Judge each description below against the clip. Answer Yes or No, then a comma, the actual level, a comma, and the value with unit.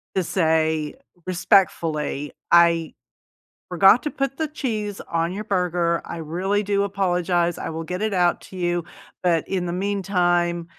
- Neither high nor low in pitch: Yes, medium, 180 Hz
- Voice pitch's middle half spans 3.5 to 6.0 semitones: No, average, 2.8 semitones